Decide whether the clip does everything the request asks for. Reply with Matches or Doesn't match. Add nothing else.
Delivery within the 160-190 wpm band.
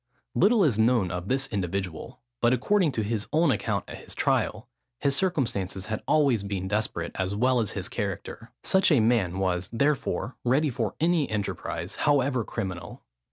Matches